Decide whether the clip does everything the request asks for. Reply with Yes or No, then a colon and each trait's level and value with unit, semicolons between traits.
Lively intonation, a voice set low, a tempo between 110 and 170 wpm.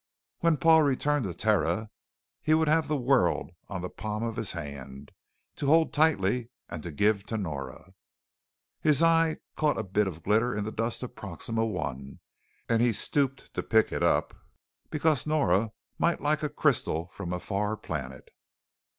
Yes: wide, 8.5 semitones; low, 110 Hz; average, 165 wpm